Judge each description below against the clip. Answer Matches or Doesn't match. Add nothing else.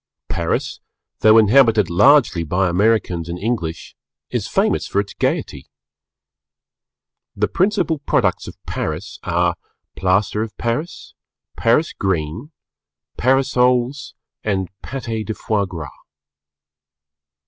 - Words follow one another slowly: Matches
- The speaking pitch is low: Matches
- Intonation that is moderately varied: Doesn't match